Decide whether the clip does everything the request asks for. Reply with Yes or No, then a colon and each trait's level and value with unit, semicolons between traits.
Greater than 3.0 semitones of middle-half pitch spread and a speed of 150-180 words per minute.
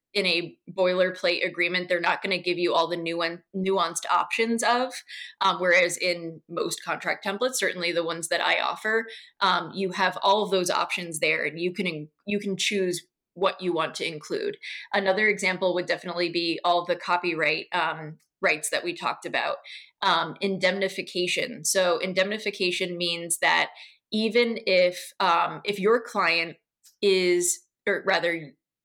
No: narrow, 2.6 semitones; average, 155 wpm